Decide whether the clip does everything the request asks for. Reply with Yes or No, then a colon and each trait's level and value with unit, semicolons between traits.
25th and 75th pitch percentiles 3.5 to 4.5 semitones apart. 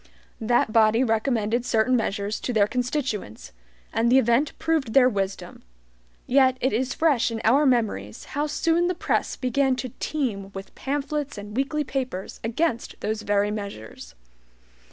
Yes: average, 4.1 semitones